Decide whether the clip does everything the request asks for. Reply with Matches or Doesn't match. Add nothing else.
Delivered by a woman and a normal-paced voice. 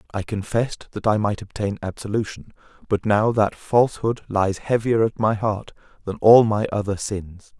Doesn't match